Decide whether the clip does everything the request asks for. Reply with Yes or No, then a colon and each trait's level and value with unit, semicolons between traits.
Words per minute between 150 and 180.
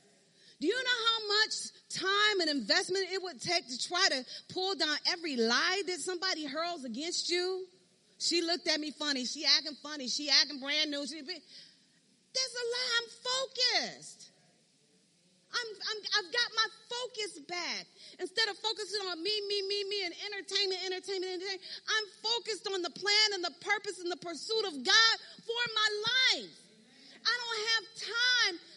Yes: average, 165 wpm